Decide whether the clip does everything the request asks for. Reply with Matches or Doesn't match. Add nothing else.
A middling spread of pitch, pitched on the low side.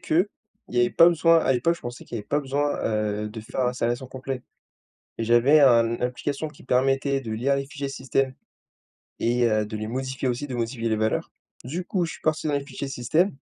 Matches